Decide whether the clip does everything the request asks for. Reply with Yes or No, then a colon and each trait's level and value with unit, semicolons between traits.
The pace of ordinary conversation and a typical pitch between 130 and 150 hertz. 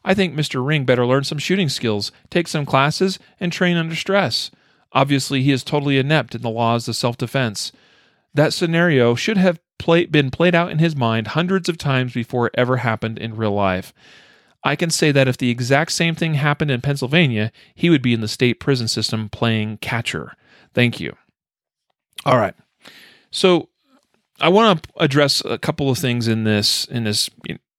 Yes: average, 190 wpm; low, 135 Hz